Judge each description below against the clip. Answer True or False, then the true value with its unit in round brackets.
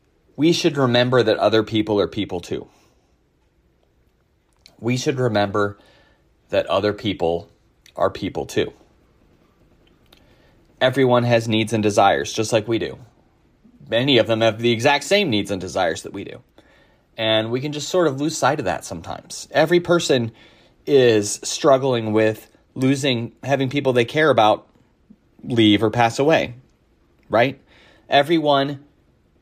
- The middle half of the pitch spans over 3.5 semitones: True (4.3 semitones)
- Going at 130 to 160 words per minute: True (140 wpm)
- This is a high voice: False (120 Hz)